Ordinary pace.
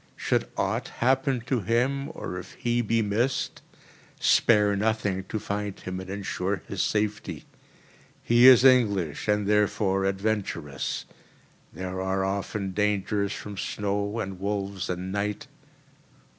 No: slow, 130 wpm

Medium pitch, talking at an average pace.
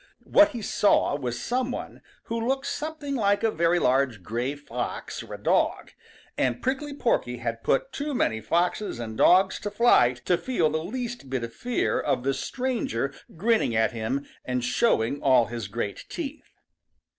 Yes: medium, 160 Hz; average, 170 wpm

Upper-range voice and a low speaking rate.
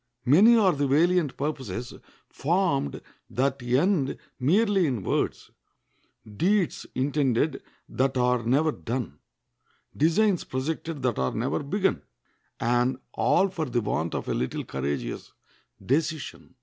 No: medium, 140 Hz; slow, 120 wpm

